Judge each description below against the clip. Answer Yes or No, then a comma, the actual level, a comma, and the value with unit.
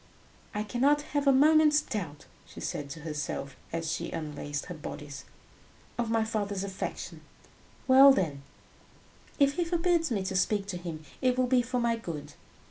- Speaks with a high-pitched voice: Yes, high, 210 Hz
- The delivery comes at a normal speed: Yes, average, 165 wpm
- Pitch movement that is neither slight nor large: No, wide, 8.6 semitones